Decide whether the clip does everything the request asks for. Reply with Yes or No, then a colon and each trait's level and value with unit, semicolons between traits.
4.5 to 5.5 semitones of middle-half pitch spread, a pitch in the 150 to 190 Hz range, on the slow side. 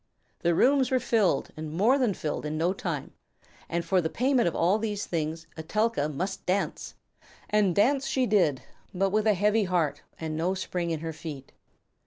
No: average, 4.8 semitones; medium, 185 Hz; average, 185 wpm